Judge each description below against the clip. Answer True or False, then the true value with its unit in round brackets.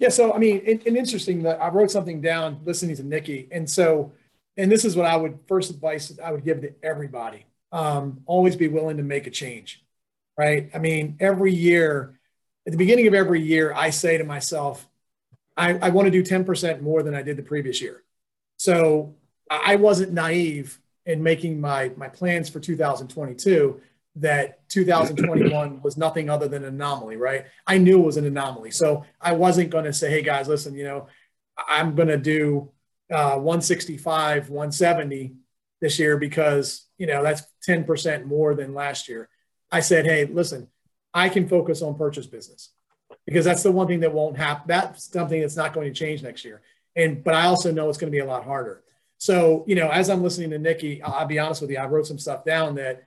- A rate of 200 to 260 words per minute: True (205 wpm)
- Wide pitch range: False (3.2 semitones)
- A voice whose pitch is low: False (155 Hz)